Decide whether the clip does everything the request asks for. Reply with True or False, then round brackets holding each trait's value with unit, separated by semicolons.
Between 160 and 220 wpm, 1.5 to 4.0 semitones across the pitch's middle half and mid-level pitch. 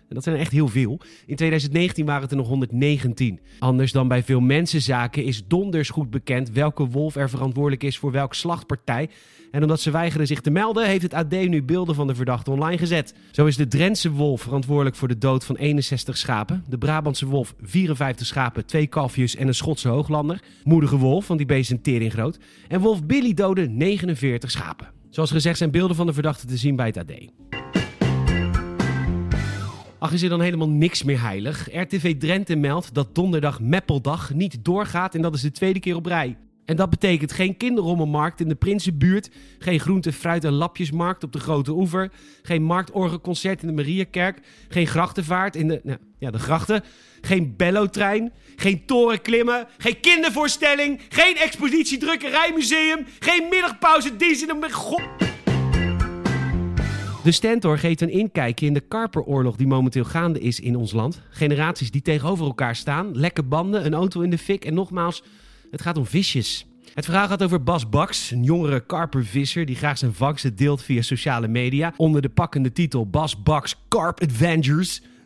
False (175 wpm; 5.1 semitones; 155 Hz)